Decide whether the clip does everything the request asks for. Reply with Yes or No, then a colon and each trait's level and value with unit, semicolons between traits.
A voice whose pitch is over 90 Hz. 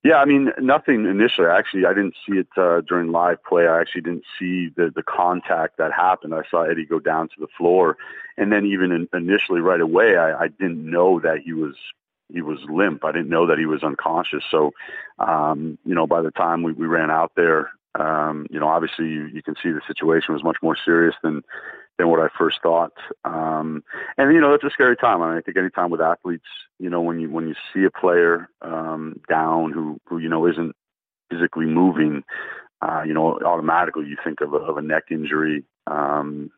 No: very low, 80 Hz